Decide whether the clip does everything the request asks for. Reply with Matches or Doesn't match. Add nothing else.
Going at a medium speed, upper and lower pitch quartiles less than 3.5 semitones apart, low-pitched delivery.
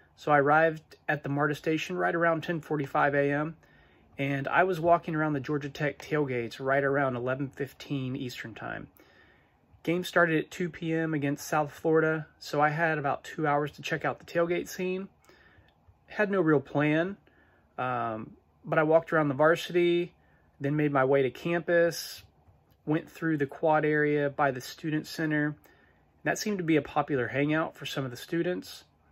Doesn't match